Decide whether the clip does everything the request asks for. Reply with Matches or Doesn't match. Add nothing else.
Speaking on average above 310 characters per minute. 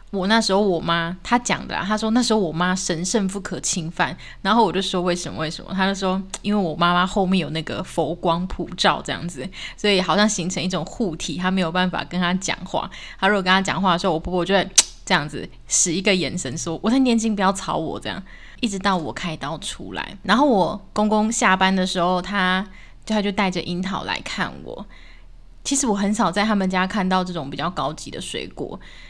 Matches